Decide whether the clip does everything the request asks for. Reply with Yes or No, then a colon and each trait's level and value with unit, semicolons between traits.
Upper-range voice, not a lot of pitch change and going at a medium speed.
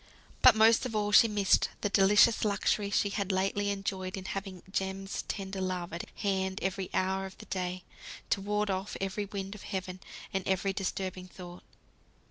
Yes: high, 195 Hz; narrow, 1.3 semitones; average, 175 wpm